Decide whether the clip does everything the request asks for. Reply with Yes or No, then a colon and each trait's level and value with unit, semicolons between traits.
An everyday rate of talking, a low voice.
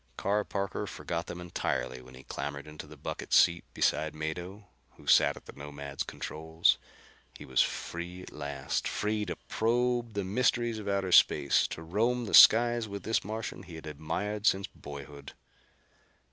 Yes: average, 165 wpm; very low, 90 Hz